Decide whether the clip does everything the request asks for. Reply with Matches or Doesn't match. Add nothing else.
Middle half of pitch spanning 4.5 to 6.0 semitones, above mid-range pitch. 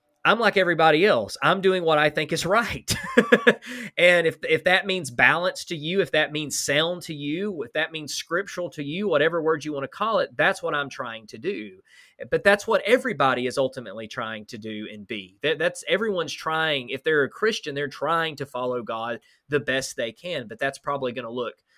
Doesn't match